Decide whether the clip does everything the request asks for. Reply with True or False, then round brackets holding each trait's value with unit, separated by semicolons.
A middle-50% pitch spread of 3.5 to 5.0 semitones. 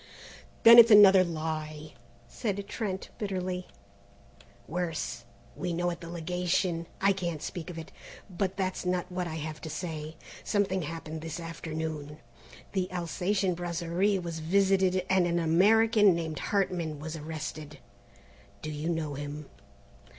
False (3.0 semitones)